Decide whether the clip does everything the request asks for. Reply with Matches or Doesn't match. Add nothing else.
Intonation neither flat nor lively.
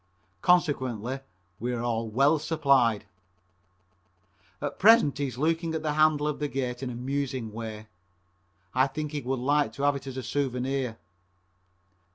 Matches